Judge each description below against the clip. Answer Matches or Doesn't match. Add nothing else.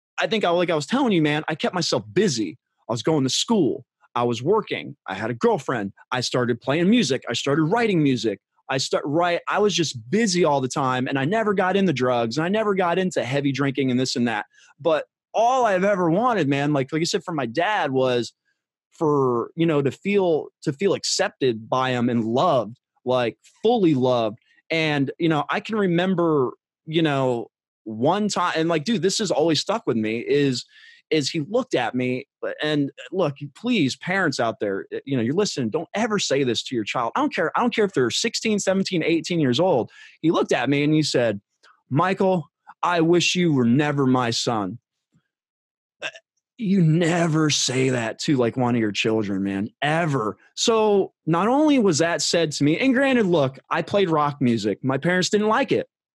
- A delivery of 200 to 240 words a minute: Matches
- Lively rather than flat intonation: Matches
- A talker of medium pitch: Matches